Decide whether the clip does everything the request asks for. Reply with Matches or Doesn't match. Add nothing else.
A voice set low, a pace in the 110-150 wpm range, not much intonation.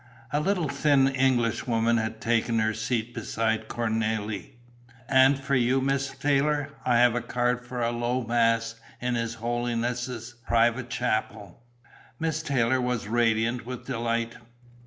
Matches